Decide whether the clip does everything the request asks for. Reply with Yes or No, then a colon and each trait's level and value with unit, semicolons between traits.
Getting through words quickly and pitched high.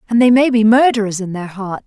Yes: fast, 260 wpm; high, 220 Hz